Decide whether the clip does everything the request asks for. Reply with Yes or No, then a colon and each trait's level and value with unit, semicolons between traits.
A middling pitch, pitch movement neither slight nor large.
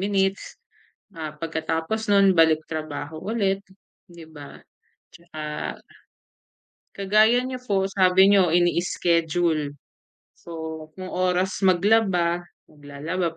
Yes: medium, 175 Hz; average, 3.2 semitones